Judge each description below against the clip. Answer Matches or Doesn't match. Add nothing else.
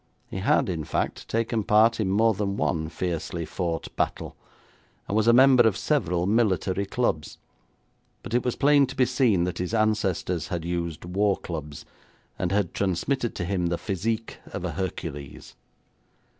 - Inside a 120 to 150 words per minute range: Doesn't match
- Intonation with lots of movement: Doesn't match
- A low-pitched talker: Matches